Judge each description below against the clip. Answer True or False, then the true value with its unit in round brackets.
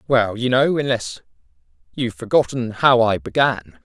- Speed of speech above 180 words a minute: False (140 wpm)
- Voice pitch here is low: True (115 Hz)